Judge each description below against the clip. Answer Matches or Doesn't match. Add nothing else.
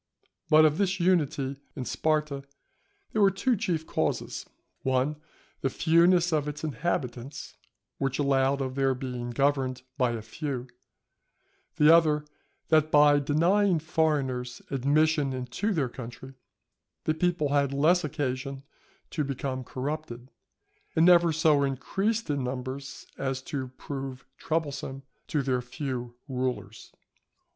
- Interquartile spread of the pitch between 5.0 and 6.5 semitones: Doesn't match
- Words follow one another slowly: Matches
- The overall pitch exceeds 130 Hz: Matches